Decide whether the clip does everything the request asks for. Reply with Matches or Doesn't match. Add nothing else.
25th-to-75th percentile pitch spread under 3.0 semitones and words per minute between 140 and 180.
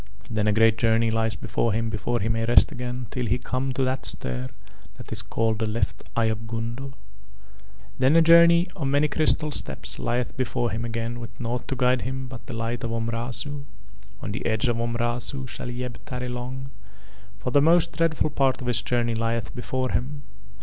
Doesn't match